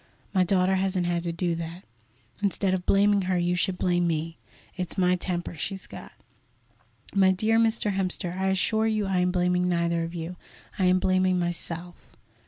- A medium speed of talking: Yes, average, 180 wpm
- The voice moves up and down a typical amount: No, narrow, 1.7 semitones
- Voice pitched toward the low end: No, medium, 180 Hz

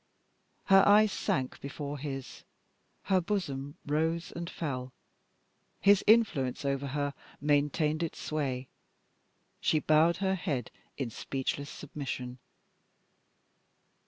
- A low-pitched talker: No, medium, 150 Hz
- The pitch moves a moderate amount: Yes, average, 3.8 semitones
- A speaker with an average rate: No, slow, 105 wpm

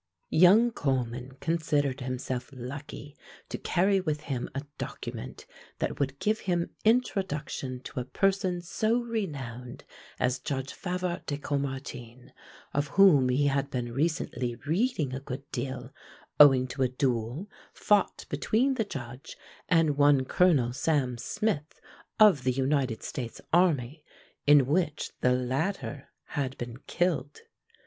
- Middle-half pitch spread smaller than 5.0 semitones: No, average, 5.3 semitones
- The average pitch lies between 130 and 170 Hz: Yes, medium, 140 Hz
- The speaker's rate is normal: No, slow, 130 wpm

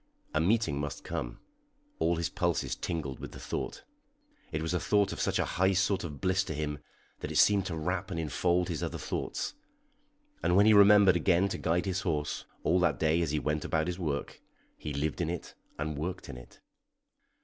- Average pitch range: Yes, average, 3.5 semitones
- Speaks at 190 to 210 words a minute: Yes, fast, 205 wpm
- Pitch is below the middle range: Yes, very low, 85 Hz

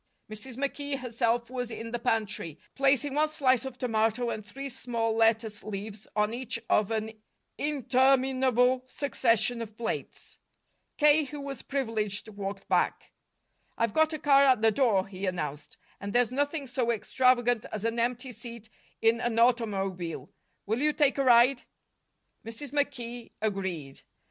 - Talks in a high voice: Yes, high, 235 Hz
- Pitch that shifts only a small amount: No, average, 3.5 semitones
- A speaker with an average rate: Yes, average, 150 wpm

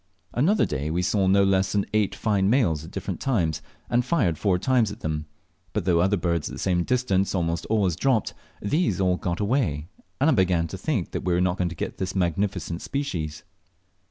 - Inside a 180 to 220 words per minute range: Yes, average, 200 wpm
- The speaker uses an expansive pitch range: No, average, 3.9 semitones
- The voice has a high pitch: No, very low, 95 Hz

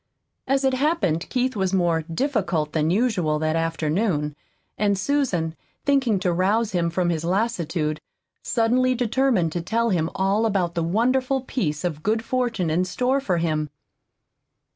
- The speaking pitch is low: No, high, 190 Hz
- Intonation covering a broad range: Yes, wide, 6.8 semitones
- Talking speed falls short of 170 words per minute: Yes, average, 150 wpm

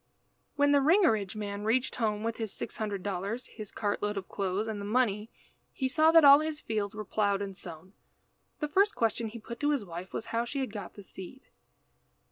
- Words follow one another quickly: Yes, fast, 215 wpm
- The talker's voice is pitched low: No, high, 215 Hz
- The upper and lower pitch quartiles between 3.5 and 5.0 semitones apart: Yes, average, 4.5 semitones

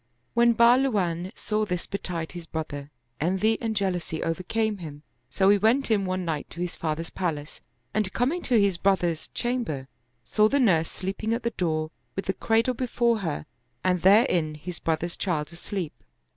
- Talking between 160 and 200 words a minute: Yes, average, 170 wpm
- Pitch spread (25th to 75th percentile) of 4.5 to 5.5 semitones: Yes, average, 5.1 semitones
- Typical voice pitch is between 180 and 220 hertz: Yes, medium, 185 Hz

